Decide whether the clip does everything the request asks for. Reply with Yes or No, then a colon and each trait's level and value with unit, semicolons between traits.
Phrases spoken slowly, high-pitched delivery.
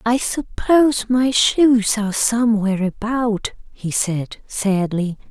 Yes: slow, 115 wpm; high, 220 Hz